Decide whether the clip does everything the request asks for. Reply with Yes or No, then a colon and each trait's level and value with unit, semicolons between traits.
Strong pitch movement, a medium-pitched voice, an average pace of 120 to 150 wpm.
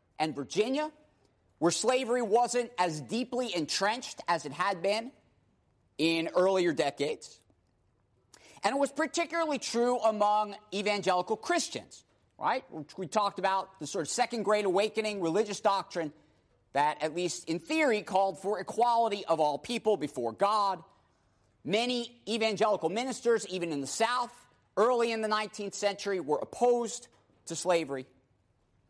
No: wide, 6.3 semitones; high, 200 Hz; slow, 135 wpm